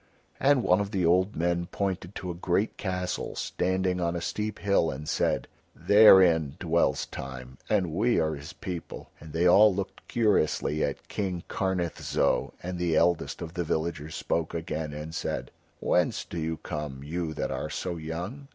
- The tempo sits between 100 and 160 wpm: No, average, 175 wpm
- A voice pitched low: Yes, very low, 85 Hz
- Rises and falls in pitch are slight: No, average, 3.0 semitones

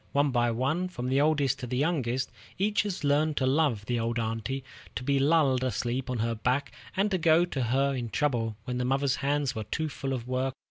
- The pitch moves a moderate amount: Yes, average, 3.1 semitones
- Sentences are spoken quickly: Yes, fast, 220 wpm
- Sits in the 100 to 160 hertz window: Yes, low, 135 Hz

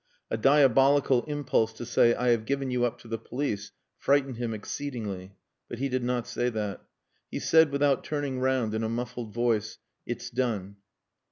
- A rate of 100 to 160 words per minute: No, average, 175 wpm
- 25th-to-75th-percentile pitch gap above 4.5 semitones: No, average, 3.3 semitones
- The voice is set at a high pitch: No, low, 120 Hz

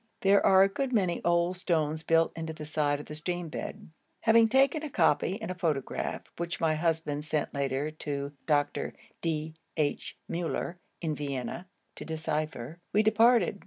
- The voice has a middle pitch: Yes, medium, 165 Hz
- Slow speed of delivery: No, average, 165 wpm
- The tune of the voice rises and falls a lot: No, average, 3.5 semitones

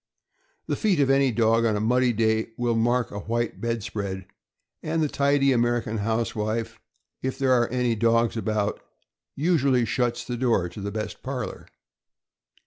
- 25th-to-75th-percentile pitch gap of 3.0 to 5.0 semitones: No, narrow, 2.5 semitones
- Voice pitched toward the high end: No, low, 115 Hz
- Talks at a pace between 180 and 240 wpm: No, average, 160 wpm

